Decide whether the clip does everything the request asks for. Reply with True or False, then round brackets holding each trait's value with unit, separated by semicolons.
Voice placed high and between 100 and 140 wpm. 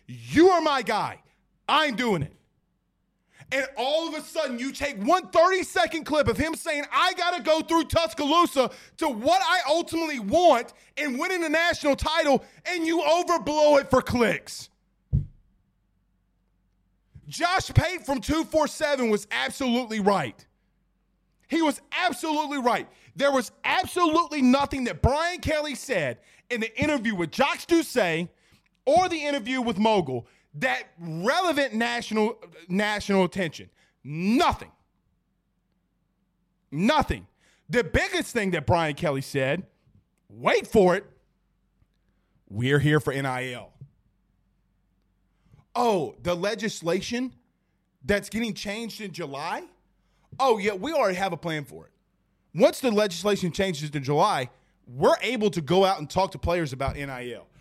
True (240 Hz; 135 wpm)